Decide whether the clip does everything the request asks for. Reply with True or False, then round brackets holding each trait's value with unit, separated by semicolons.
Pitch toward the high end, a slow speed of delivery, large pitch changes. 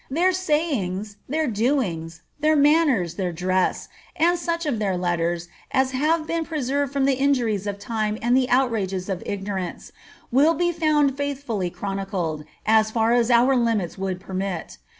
False (235 Hz; 155 wpm; 6.9 semitones)